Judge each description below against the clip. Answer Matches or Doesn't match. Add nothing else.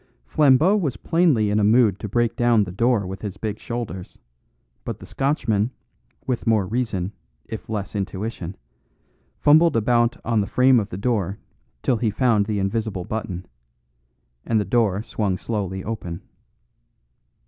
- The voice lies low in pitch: Matches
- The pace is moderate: Matches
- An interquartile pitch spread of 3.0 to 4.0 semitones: Matches